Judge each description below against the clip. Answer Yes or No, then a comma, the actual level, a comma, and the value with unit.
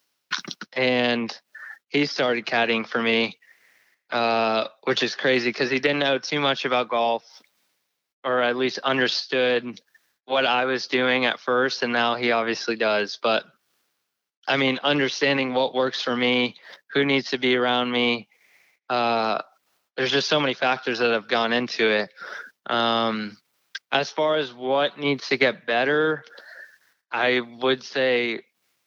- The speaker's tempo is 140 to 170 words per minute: Yes, average, 145 wpm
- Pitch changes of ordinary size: No, narrow, 2.1 semitones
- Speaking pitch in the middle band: No, low, 125 Hz